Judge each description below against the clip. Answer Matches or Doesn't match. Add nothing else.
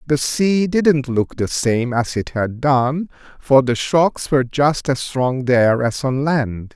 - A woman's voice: Doesn't match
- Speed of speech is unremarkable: Matches